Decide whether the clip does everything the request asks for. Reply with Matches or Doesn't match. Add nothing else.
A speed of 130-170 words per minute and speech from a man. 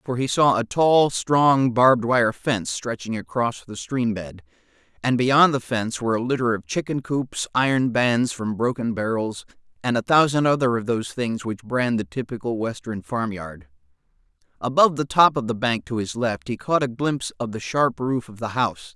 Doesn't match